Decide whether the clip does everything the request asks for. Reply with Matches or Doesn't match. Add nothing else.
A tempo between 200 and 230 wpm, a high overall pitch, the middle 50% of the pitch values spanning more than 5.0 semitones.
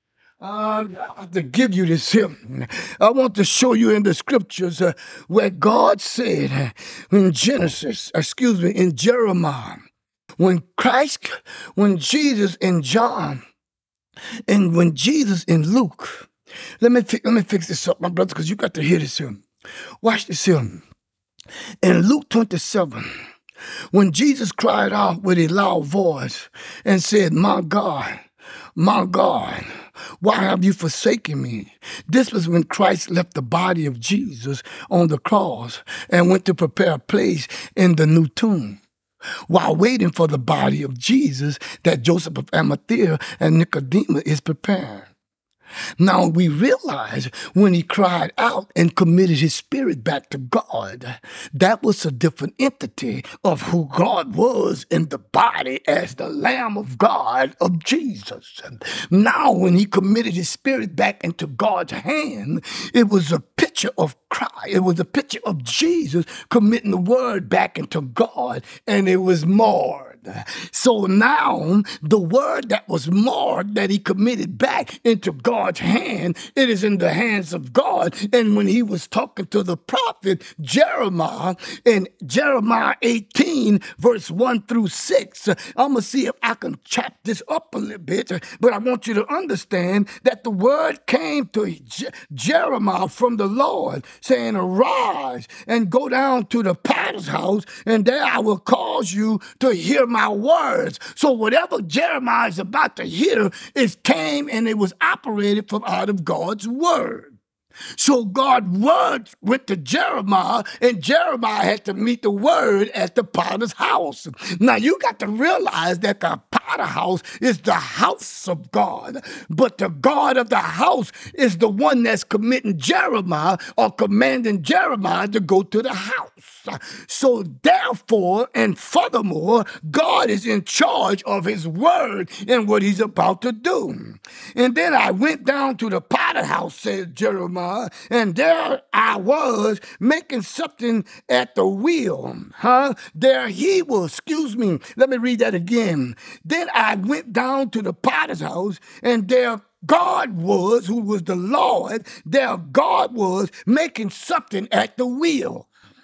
Doesn't match